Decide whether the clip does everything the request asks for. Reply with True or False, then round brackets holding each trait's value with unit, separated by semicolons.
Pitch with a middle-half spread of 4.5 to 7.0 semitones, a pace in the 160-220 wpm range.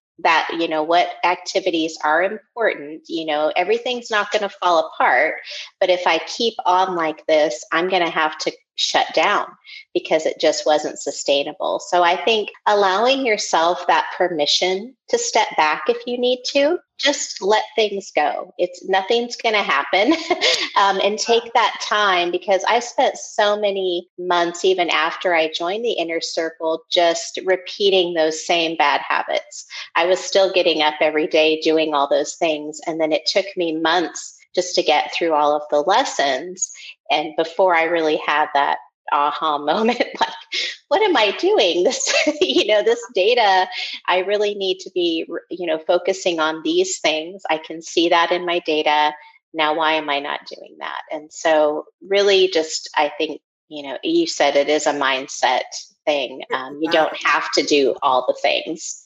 True (5.2 semitones; 175 wpm)